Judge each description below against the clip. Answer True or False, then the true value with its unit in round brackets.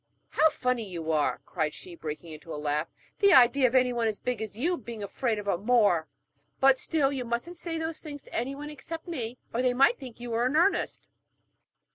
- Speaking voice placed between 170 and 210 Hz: False (245 Hz)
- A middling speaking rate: False (210 wpm)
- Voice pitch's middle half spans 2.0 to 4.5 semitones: False (5.6 semitones)